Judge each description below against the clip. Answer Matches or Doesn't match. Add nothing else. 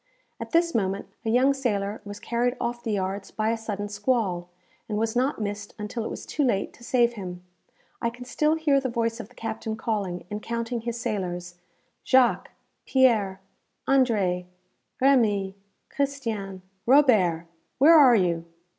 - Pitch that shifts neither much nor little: Matches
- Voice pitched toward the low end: Doesn't match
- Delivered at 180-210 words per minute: Doesn't match